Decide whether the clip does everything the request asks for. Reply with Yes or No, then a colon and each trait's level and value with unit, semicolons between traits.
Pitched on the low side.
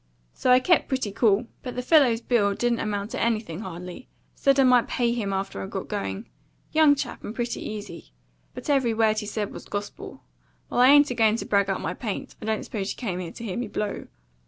No: high, 220 Hz